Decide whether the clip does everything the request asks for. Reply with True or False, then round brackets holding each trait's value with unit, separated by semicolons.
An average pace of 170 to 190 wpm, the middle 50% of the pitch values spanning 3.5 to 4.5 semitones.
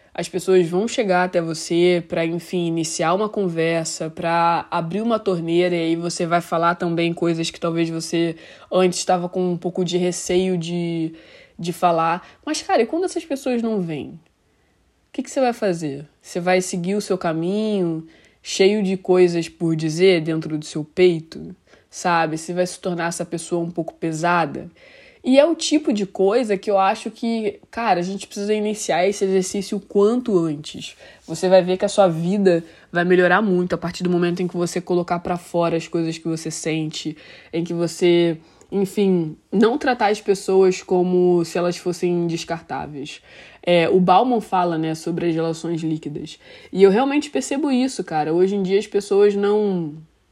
False (180 wpm; 2.8 semitones)